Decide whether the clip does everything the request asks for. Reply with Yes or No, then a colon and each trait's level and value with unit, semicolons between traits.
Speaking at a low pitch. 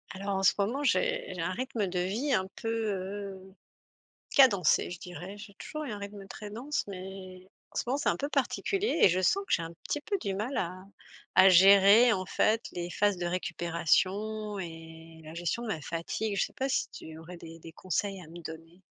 No: high, 195 Hz